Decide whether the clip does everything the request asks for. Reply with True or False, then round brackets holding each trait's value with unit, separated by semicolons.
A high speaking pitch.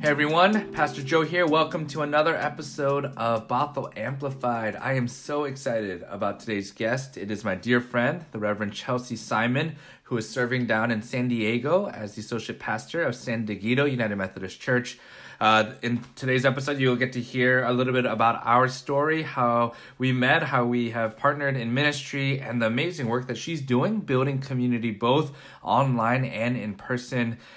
False (125 Hz)